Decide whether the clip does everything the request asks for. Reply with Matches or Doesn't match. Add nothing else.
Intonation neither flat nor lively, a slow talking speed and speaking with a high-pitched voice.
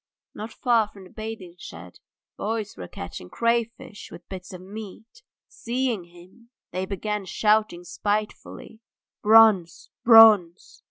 Matches